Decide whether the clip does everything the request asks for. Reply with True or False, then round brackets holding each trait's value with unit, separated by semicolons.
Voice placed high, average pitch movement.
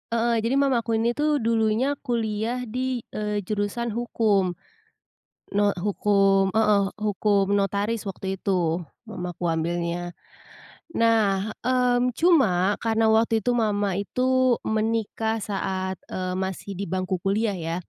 True (210 Hz; 3.1 semitones)